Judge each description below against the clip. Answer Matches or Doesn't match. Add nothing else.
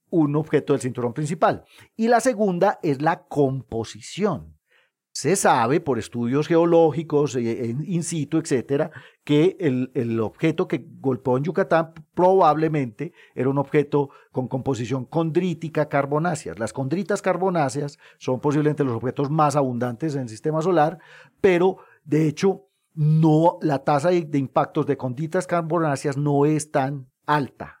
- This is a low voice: Doesn't match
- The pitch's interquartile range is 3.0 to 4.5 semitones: Matches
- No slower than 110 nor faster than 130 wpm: Doesn't match